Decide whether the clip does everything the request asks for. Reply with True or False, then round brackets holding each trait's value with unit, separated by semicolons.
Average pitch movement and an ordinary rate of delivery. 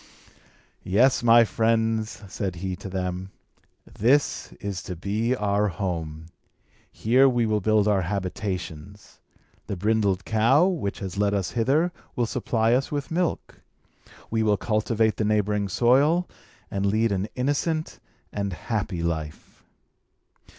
False (3.5 semitones; 130 wpm)